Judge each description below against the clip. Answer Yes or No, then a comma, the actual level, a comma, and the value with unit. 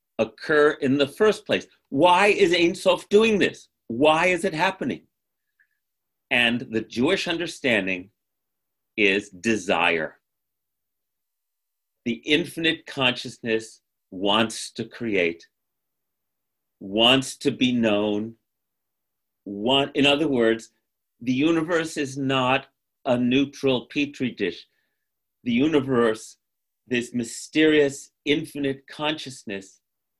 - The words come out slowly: Yes, slow, 95 wpm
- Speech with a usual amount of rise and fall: No, wide, 5.7 semitones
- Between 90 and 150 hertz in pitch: Yes, low, 135 Hz